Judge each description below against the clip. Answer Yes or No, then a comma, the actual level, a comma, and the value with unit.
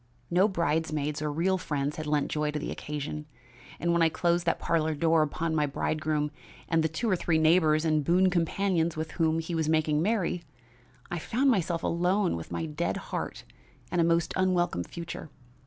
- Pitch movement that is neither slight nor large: No, narrow, 2.3 semitones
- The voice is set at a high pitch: No, medium, 160 Hz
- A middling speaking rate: Yes, average, 190 wpm